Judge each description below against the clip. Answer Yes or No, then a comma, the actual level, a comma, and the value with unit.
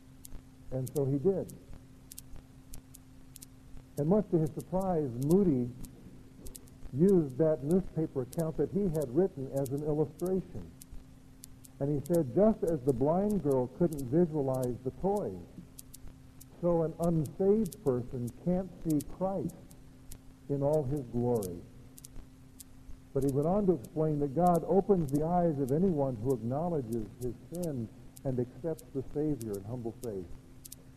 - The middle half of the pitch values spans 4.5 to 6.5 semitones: Yes, average, 5.2 semitones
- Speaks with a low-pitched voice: No, medium, 145 Hz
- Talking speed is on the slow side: Yes, slow, 130 wpm